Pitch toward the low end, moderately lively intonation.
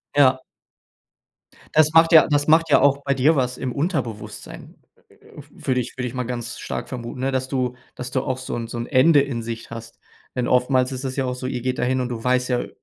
No: low, 130 Hz; narrow, 1.9 semitones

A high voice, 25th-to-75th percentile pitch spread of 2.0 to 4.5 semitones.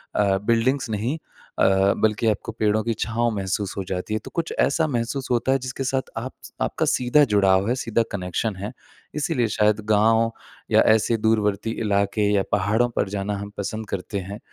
No: low, 110 Hz; average, 2.7 semitones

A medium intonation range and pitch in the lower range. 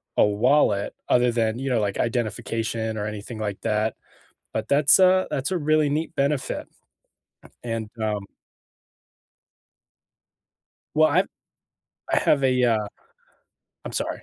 Yes: average, 4.5 semitones; low, 115 Hz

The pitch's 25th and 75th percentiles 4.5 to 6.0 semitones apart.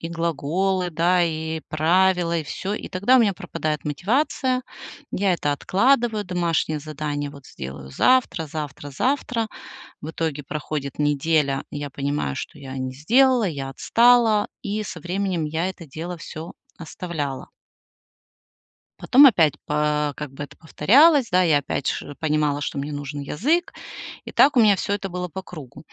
Yes: average, 5.3 semitones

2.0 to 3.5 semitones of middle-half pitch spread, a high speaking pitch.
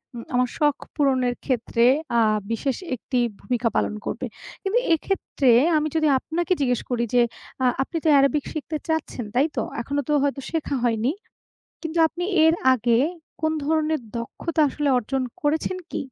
No: average, 4.2 semitones; very high, 280 Hz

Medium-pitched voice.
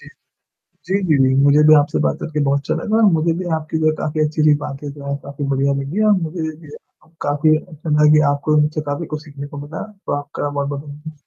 Yes: medium, 150 Hz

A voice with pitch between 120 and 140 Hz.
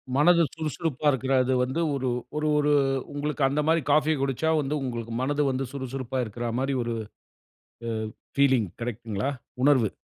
Yes: low, 135 Hz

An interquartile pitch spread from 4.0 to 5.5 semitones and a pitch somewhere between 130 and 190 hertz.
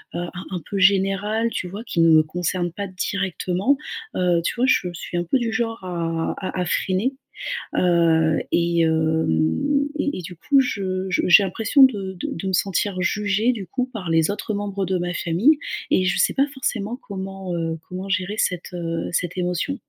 No: average, 3.2 semitones; medium, 185 Hz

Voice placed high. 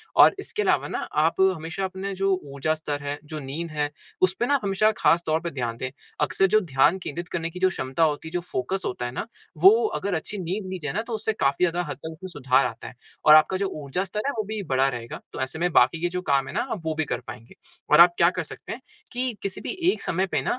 No: medium, 165 Hz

